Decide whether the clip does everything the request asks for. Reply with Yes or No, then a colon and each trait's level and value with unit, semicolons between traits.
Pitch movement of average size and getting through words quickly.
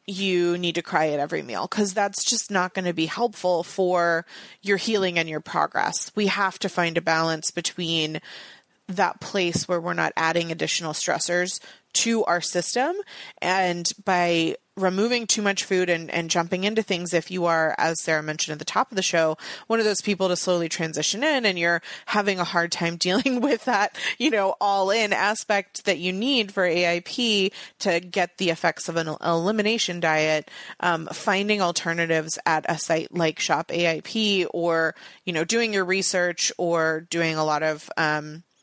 No: average, 3.2 semitones; average, 185 wpm